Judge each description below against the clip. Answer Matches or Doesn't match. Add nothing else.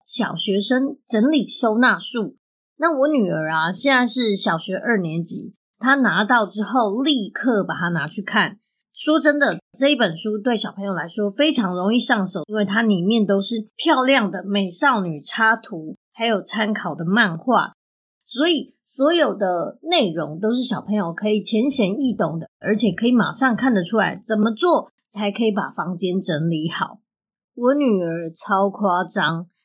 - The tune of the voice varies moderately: Matches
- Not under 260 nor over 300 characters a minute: Doesn't match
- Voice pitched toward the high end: Matches